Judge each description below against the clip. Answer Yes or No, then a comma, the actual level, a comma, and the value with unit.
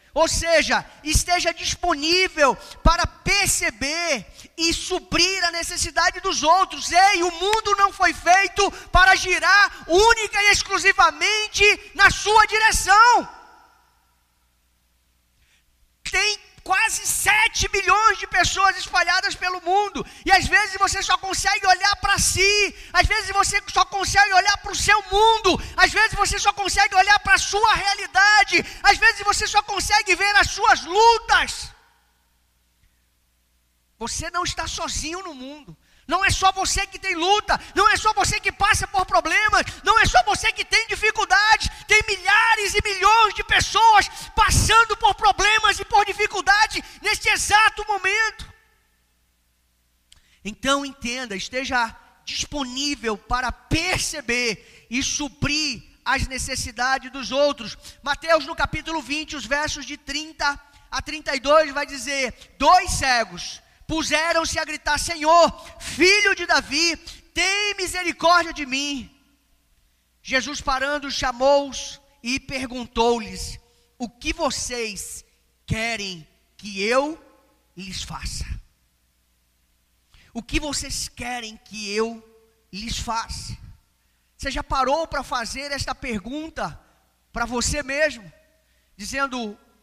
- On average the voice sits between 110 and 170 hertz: No, very high, 335 Hz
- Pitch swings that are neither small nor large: No, wide, 7.3 semitones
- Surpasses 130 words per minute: No, average, 125 wpm